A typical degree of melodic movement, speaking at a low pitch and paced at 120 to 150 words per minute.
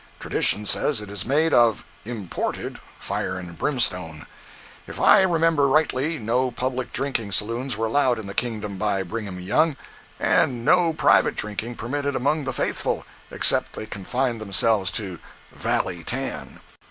Yes: average, 5.0 semitones; low, 115 Hz; average, 145 wpm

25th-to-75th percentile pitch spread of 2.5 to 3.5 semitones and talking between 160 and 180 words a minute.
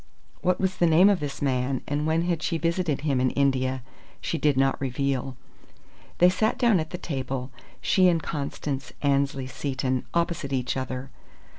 No: average, 4.3 semitones; average, 170 wpm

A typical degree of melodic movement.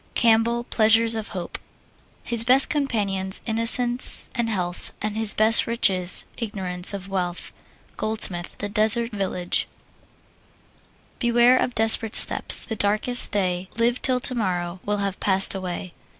Yes: average, 3.6 semitones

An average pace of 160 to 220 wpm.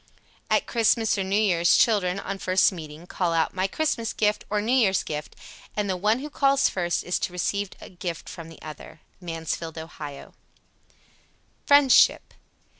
Yes: average, 165 wpm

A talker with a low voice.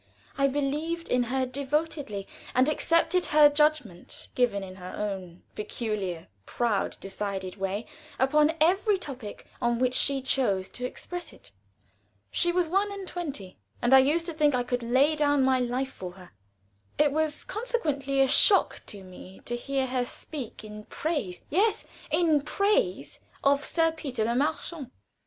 No: very high, 270 Hz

